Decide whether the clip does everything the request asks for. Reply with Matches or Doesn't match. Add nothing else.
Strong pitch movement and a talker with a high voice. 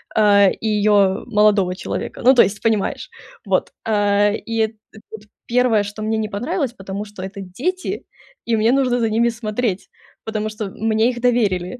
Doesn't match